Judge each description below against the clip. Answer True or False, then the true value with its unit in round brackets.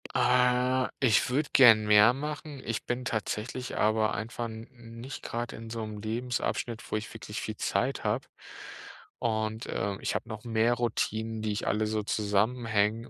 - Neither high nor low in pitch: False (115 Hz)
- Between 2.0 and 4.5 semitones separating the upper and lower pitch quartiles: True (2.4 semitones)